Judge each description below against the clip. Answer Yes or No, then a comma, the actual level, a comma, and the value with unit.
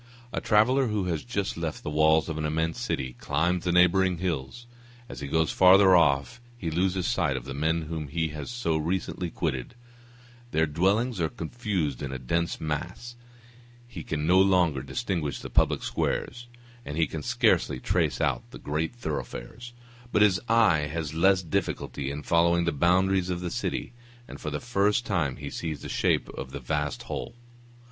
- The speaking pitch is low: Yes, very low, 85 Hz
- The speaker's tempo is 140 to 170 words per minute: No, average, 180 wpm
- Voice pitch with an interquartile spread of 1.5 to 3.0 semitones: No, average, 4.0 semitones